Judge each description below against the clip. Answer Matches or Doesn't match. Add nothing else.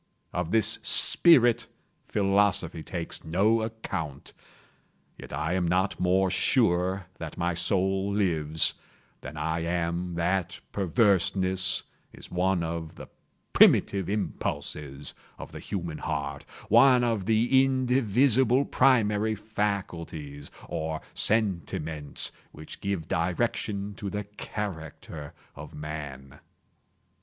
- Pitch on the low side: Matches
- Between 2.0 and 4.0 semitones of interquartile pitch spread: Doesn't match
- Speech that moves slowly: Matches